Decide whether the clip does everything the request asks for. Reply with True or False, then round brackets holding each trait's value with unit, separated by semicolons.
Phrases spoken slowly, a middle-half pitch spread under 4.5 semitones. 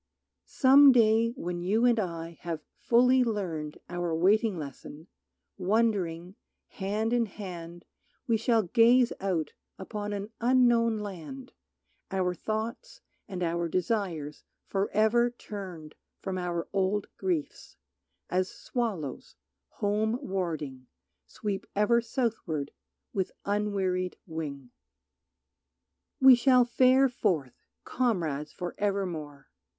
False (105 wpm; 5.2 semitones)